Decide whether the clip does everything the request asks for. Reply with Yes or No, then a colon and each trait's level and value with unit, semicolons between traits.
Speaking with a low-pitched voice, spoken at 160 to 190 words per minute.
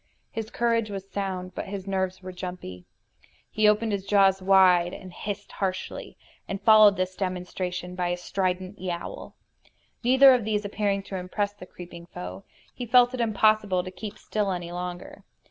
No: high, 190 Hz; average, 165 wpm